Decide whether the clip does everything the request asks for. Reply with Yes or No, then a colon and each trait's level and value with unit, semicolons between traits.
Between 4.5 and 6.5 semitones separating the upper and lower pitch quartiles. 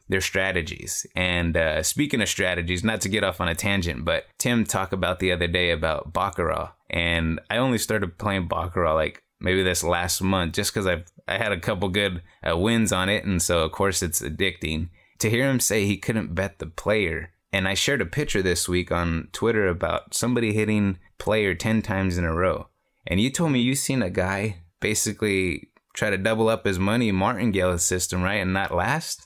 No: average, 3.4 semitones